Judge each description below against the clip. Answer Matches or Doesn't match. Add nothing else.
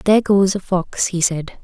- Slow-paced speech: Doesn't match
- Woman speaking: Matches